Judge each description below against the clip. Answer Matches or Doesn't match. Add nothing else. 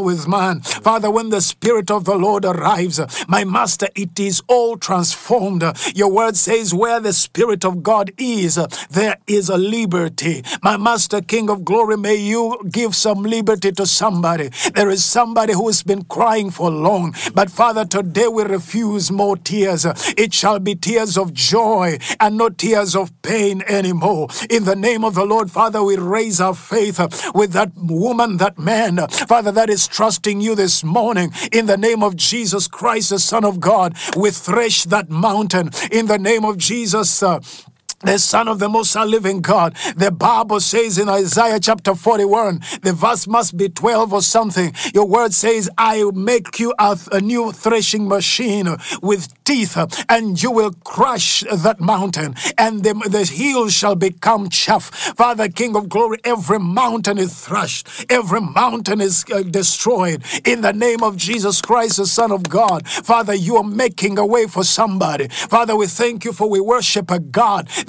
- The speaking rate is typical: Matches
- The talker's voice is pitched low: Doesn't match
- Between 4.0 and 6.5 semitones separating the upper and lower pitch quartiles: Doesn't match